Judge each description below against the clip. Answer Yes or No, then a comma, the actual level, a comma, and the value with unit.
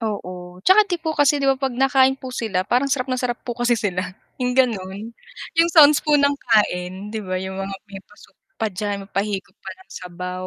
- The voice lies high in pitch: Yes, high, 220 Hz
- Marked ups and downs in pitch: Yes, wide, 5.8 semitones